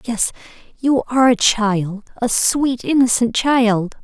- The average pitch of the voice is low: No, high, 235 Hz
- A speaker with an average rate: No, slow, 120 wpm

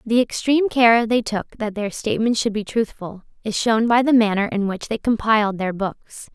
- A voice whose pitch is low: No, high, 220 Hz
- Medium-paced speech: No, fast, 210 wpm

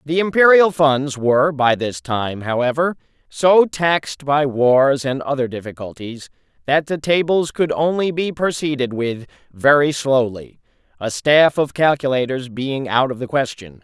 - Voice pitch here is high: No, medium, 140 Hz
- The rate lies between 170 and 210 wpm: No, average, 145 wpm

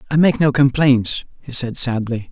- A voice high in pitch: No, low, 130 Hz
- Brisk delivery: No, average, 180 wpm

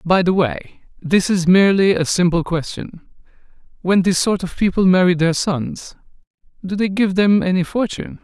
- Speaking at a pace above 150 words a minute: Yes, average, 170 wpm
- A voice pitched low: No, medium, 185 Hz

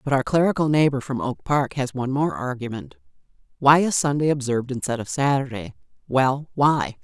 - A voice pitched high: No, medium, 140 Hz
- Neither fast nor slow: Yes, average, 170 wpm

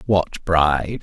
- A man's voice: Yes, male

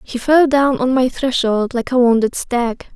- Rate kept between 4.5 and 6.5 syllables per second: No, 4.3 syllables/s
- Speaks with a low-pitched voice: No, very high, 250 Hz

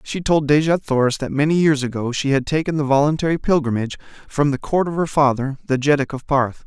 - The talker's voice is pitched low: No, medium, 145 Hz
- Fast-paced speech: Yes, fast, 215 wpm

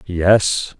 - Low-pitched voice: Yes, very low, 95 Hz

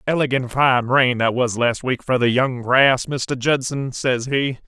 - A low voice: Yes, low, 130 Hz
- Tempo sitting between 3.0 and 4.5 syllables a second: Yes, 4.0 syllables/s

